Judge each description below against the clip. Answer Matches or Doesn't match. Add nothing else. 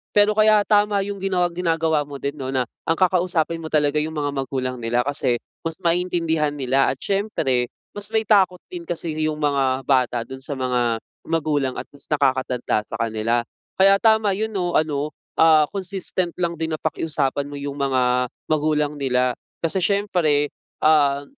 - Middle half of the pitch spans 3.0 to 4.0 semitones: Doesn't match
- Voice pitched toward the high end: Doesn't match